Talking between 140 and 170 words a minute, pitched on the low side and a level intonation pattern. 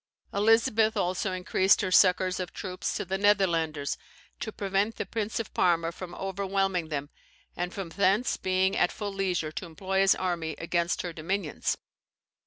No: average, 160 wpm; medium, 185 Hz; narrow, 2.3 semitones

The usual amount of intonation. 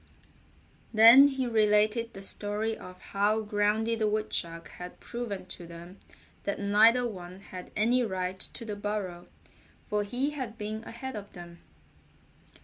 Yes: average, 3.2 semitones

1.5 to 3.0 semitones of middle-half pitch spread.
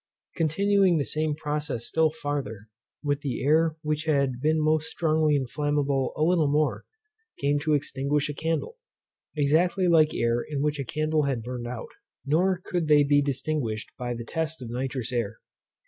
Yes: average, 2.7 semitones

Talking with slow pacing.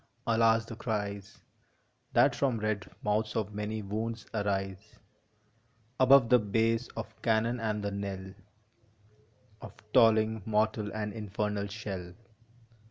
Yes: slow, 115 wpm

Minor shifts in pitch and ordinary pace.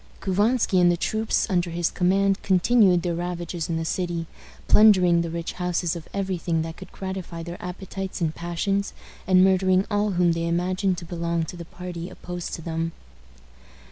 Yes: narrow, 1.9 semitones; average, 175 wpm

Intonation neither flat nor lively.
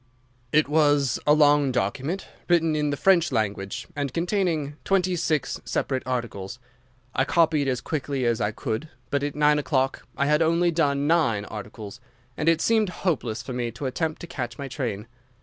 Yes: average, 4.6 semitones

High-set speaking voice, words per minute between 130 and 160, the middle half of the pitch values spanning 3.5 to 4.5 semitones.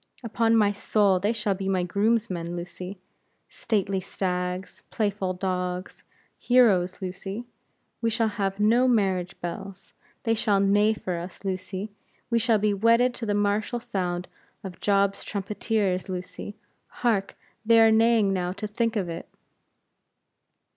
No: high, 200 Hz; average, 140 wpm; average, 3.1 semitones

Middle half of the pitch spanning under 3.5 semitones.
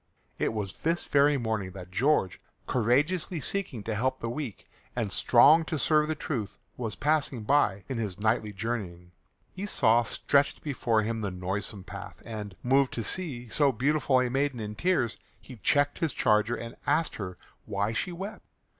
No: wide, 5.4 semitones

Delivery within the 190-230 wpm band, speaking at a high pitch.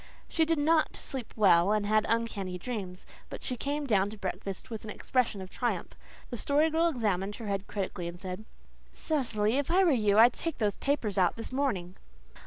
Yes: average, 195 wpm; high, 220 Hz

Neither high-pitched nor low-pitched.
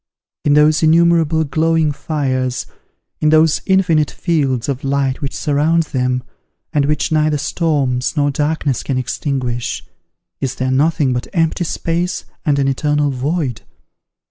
Yes: medium, 150 Hz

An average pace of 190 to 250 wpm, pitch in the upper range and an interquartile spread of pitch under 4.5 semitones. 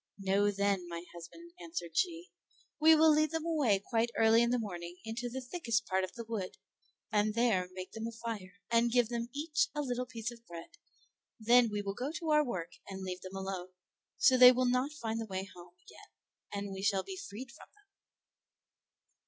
No: average, 200 wpm; high, 230 Hz; average, 4.9 semitones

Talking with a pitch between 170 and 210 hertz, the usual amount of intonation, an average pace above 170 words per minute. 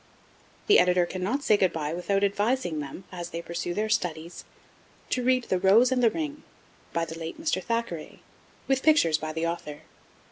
No: medium, 185 Hz; wide, 6.6 semitones; average, 180 wpm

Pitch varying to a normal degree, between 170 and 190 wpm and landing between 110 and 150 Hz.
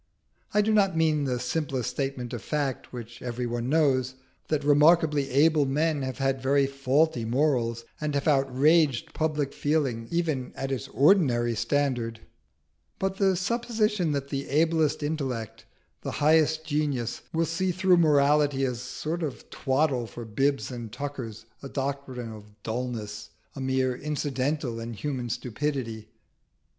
No: average, 3.7 semitones; average, 145 wpm; medium, 140 Hz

